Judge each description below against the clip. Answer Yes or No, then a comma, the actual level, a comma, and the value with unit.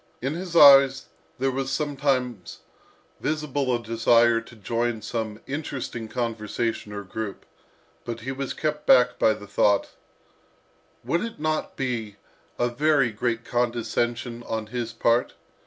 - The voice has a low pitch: Yes, low, 120 Hz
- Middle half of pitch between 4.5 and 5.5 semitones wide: No, average, 3.0 semitones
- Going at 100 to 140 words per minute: Yes, slow, 135 wpm